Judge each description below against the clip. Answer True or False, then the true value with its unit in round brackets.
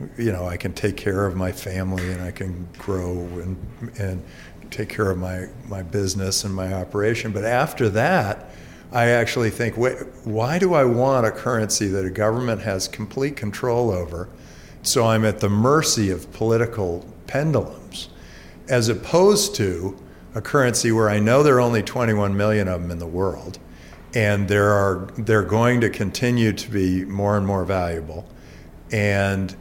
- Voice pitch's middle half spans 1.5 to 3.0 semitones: False (3.6 semitones)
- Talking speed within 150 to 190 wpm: True (170 wpm)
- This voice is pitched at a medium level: False (100 Hz)